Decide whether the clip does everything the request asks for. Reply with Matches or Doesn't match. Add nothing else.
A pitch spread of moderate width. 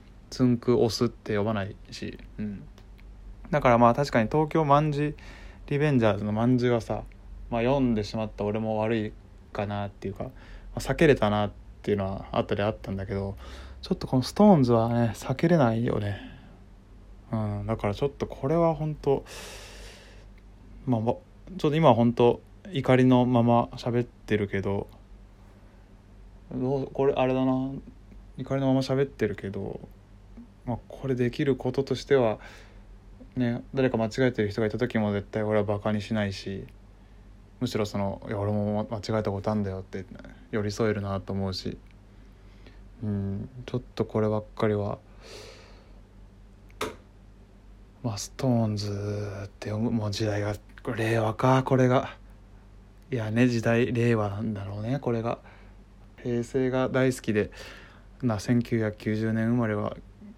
Matches